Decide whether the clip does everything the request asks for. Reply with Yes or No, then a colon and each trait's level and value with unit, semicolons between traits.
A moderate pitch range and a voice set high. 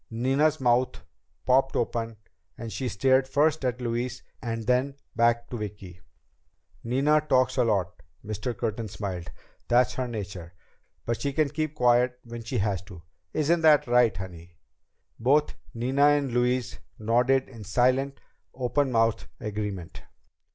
No: average, 3.5 semitones; low, 120 Hz